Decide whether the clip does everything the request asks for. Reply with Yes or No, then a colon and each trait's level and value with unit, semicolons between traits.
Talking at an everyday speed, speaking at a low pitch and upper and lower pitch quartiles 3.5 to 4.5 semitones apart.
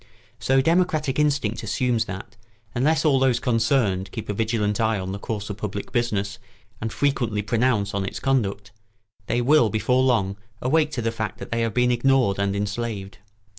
Yes: average, 175 wpm; low, 115 Hz; average, 4.2 semitones